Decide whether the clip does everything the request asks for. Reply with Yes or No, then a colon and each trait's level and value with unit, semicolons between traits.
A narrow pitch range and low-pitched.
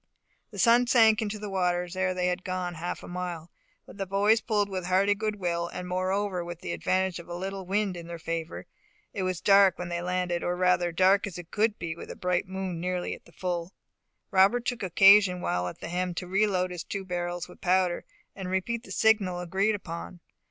No: narrow, 2.1 semitones; medium, 185 Hz